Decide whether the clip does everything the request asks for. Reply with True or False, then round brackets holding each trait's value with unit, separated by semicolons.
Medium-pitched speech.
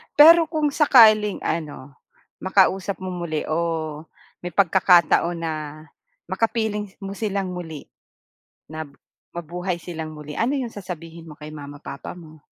True (175 Hz)